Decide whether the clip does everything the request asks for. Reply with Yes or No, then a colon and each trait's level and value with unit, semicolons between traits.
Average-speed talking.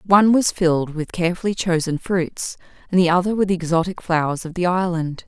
Yes: average, 195 wpm